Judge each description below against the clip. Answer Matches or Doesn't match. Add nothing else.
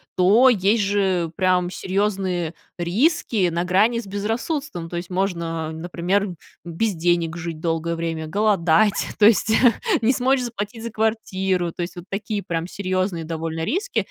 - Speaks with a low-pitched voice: Doesn't match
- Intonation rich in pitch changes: Doesn't match